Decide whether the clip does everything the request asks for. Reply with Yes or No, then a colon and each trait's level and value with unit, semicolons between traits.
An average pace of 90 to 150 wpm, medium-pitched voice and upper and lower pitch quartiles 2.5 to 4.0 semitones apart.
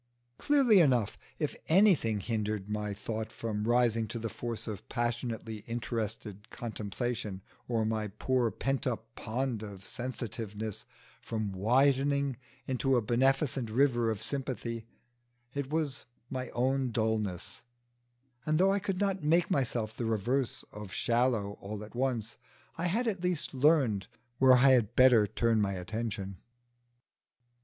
No: slow, 135 wpm; low, 120 Hz; average, 3.7 semitones